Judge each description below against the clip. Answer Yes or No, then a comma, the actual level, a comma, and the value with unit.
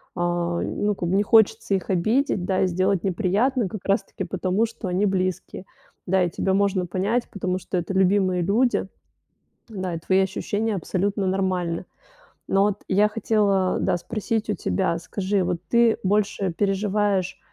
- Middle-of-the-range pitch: No, high, 195 Hz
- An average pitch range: No, narrow, 2.1 semitones